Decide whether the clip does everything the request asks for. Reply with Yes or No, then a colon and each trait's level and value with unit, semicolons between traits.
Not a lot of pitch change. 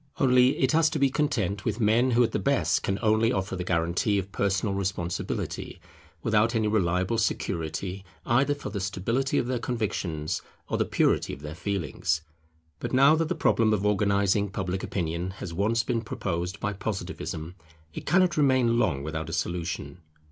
No: average, 4.9 semitones